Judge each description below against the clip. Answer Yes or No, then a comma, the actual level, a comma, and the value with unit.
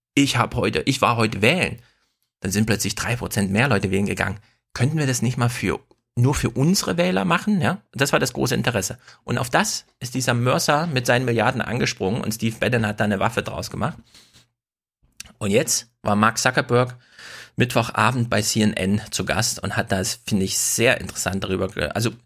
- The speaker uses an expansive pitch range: No, average, 3.3 semitones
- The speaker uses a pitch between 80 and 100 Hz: No, low, 115 Hz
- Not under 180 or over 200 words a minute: Yes, fast, 190 wpm